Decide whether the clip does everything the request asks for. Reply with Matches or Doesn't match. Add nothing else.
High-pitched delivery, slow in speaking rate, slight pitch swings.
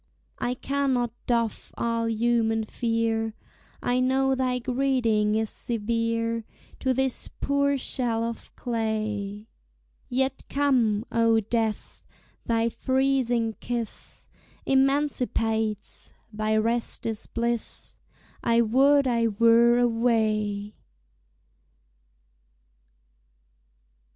Matches